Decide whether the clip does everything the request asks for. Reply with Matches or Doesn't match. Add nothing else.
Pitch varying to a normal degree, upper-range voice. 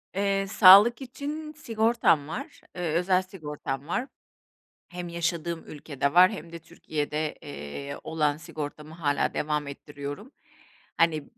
Doesn't match